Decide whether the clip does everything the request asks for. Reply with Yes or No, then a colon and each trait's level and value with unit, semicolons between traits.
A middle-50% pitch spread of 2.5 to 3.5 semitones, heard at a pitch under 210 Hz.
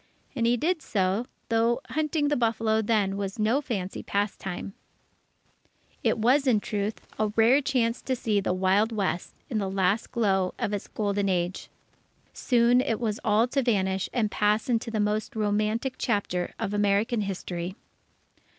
No: average, 3.0 semitones; high, 215 Hz